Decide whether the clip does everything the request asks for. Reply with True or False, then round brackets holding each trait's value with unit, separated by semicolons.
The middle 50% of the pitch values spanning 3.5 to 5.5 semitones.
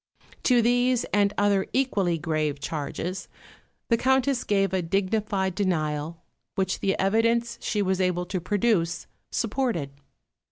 True (4.7 semitones)